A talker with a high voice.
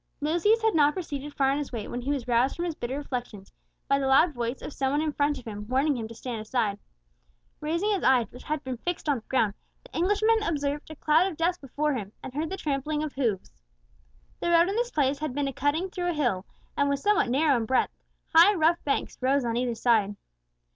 Yes: very high, 285 Hz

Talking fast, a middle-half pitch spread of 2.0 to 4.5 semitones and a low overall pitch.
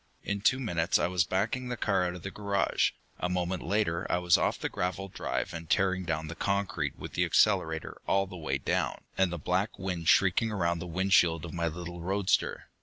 Yes: fast, 210 wpm; narrow, 2.6 semitones; very low, 90 Hz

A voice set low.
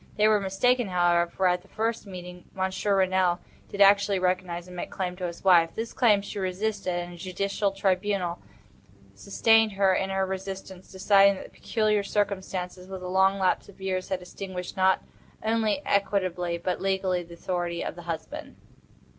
No: high, 190 Hz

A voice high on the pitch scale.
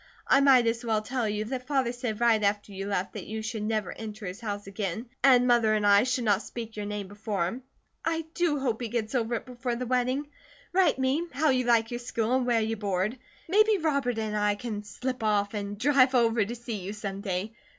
Yes: high, 225 Hz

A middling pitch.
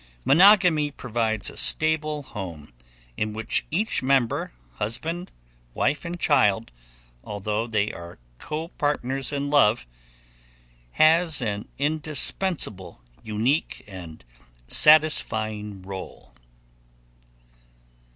No: low, 130 Hz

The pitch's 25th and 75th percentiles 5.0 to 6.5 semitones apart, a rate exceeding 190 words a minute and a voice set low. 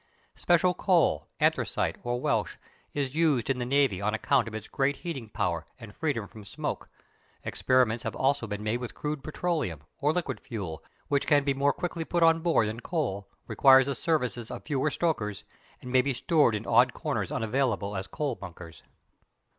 No: wide, 5.4 semitones; average, 180 wpm; low, 130 Hz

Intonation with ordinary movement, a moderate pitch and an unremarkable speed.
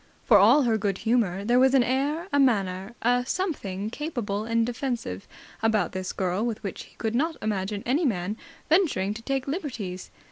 No: average, 4.9 semitones; high, 230 Hz; average, 180 wpm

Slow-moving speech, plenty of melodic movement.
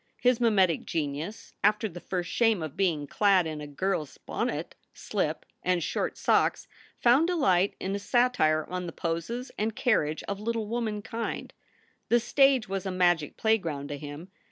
No: average, 165 wpm; wide, 5.7 semitones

